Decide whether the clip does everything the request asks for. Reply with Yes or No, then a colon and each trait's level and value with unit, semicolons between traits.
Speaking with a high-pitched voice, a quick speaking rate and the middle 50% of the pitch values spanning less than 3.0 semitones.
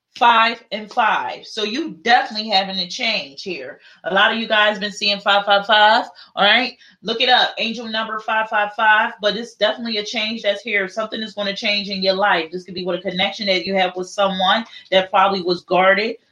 Yes: high, 210 Hz; fast, 220 wpm; narrow, 2.5 semitones